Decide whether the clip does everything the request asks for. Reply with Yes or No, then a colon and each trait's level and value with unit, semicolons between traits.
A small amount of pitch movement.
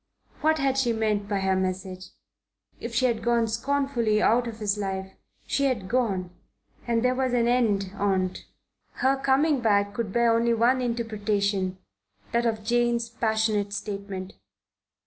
No: average, 3.2 semitones